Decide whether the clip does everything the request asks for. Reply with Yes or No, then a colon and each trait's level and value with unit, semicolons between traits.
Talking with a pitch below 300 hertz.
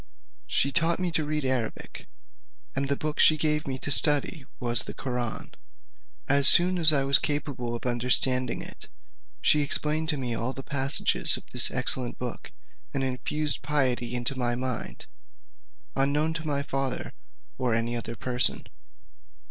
Yes: low, 135 Hz